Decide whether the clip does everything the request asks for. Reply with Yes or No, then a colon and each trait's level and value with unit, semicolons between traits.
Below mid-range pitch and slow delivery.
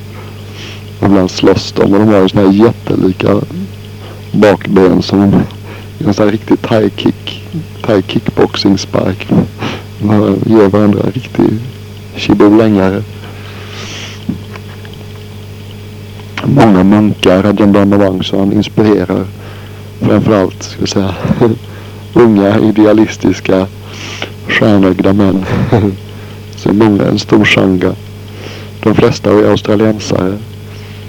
Yes: low, 105 Hz; slow, 90 wpm